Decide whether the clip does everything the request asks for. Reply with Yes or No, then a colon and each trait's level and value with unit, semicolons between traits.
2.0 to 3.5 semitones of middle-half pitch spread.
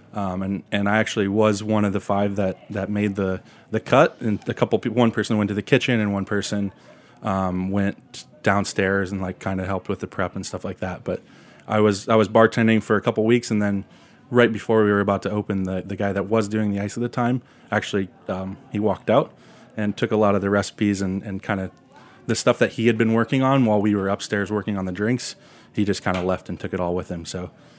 Yes: narrow, 2.4 semitones